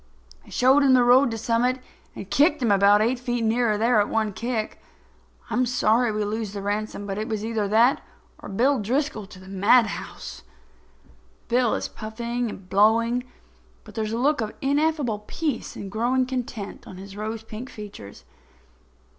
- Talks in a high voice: Yes, high, 225 Hz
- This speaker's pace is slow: No, average, 175 wpm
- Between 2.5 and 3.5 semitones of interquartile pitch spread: Yes, average, 3.0 semitones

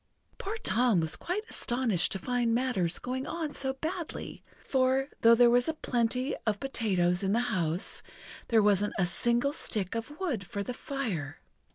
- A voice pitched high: Yes, high, 240 Hz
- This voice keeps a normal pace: Yes, average, 170 wpm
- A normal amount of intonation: Yes, average, 4.9 semitones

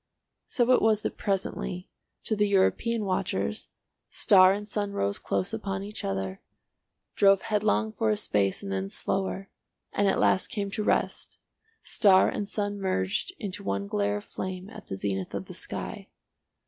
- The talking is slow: No, average, 165 wpm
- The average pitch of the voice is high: Yes, high, 195 Hz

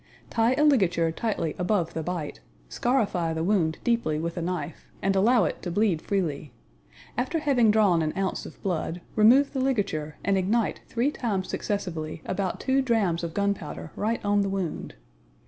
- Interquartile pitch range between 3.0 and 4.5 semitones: No, average, 5.3 semitones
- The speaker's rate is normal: Yes, average, 170 wpm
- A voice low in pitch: No, high, 195 Hz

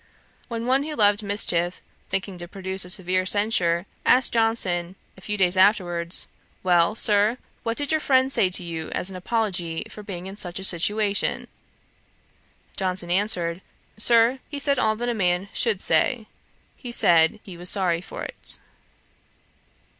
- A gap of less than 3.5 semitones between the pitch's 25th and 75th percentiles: No, average, 4.1 semitones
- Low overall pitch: No, high, 195 Hz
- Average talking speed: Yes, average, 160 wpm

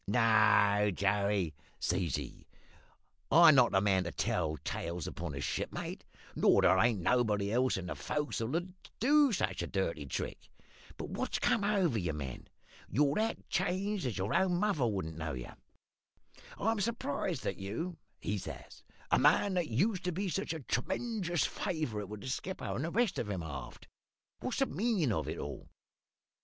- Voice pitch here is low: Yes, low, 120 Hz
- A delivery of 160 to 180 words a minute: Yes, average, 170 wpm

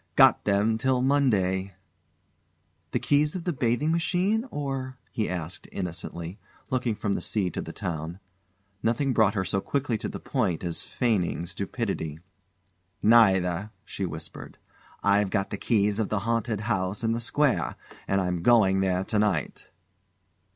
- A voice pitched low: Yes, low, 105 Hz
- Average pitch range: Yes, average, 4.7 semitones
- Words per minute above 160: No, average, 155 wpm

